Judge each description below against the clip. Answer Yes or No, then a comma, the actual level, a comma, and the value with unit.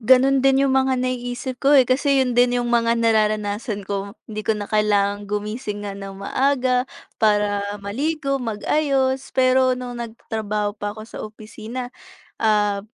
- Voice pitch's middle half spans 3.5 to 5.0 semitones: Yes, average, 3.8 semitones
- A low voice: No, high, 230 Hz